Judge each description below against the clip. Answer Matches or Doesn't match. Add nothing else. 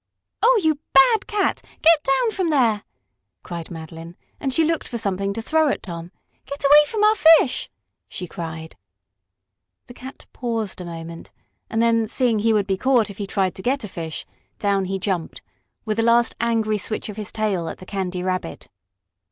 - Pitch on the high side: Matches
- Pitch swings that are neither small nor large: Doesn't match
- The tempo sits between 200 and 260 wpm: Doesn't match